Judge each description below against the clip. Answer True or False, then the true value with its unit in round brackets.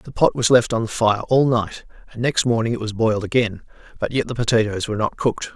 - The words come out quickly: True (250 wpm)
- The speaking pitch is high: False (115 Hz)